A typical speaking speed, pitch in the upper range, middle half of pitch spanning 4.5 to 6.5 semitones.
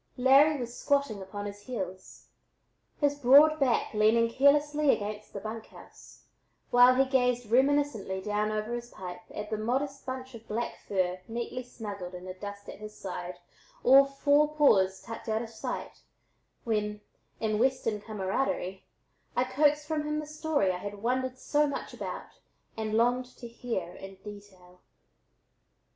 Yes: average, 155 wpm; high, 230 Hz; average, 4.8 semitones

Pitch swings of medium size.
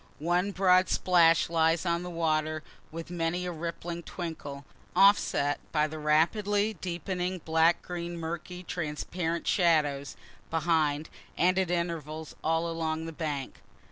No: narrow, 2.1 semitones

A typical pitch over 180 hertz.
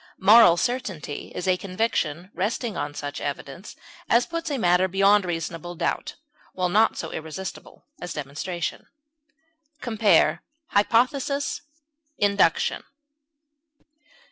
Yes: high, 190 Hz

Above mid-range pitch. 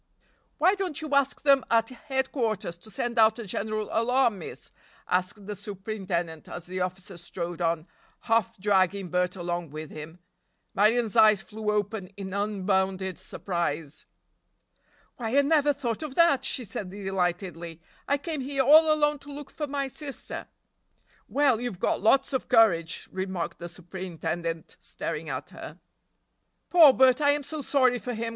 Yes: high, 215 Hz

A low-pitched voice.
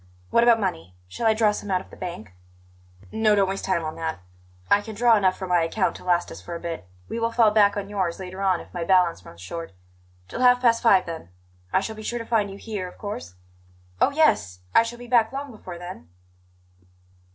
No: high, 195 Hz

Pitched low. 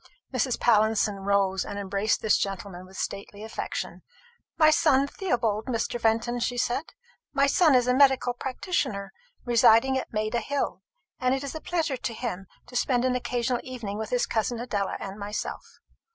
No: high, 240 Hz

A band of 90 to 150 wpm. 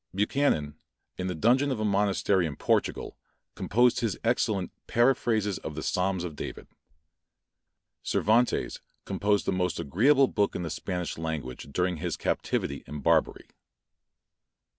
Yes: slow, 135 wpm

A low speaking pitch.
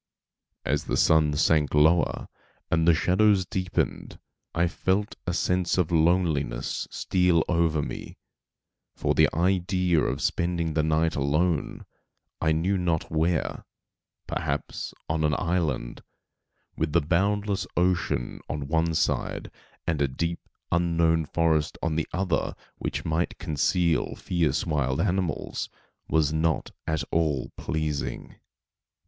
Yes: very low, 80 Hz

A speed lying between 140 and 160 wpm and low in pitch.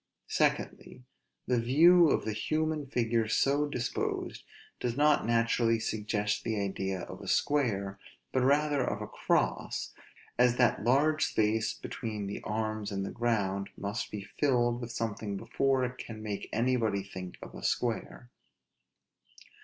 Yes: average, 145 wpm; low, 115 Hz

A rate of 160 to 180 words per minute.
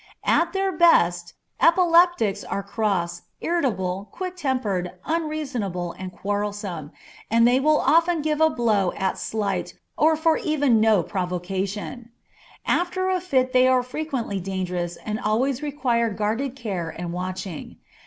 No: slow, 135 wpm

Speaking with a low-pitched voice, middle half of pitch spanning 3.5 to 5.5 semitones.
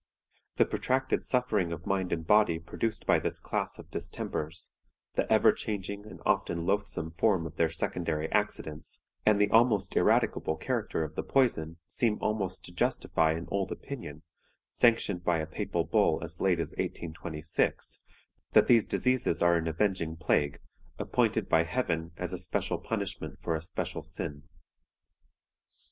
Yes: very low, 85 Hz; average, 4.3 semitones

